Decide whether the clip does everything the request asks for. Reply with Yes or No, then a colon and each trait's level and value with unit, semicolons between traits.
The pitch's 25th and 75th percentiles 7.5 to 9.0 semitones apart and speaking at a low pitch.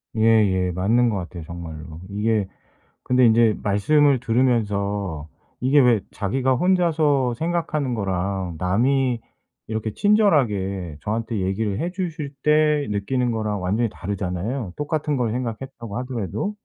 No: wide, 5.4 semitones; low, 115 Hz